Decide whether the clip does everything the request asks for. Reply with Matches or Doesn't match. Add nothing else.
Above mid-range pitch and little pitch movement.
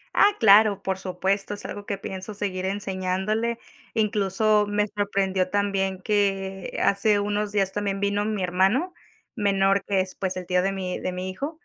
Matches